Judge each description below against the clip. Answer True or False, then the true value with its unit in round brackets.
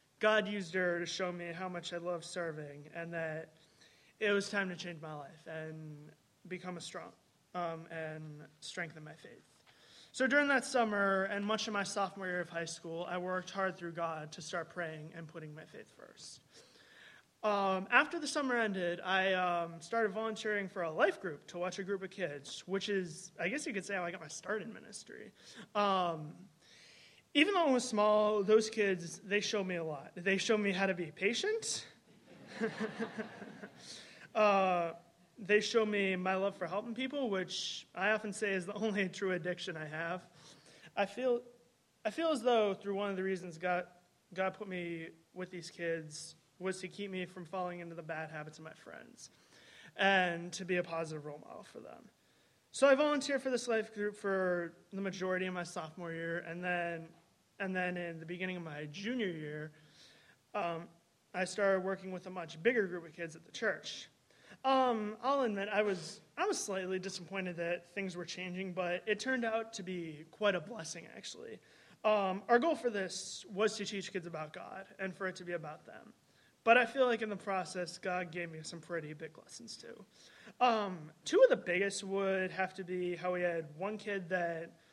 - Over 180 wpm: True (195 wpm)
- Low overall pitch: False (185 Hz)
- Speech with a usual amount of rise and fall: True (3.4 semitones)